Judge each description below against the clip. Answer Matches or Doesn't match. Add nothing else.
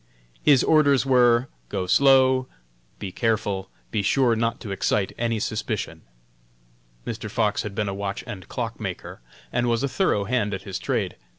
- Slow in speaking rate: Doesn't match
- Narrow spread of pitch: Doesn't match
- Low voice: Matches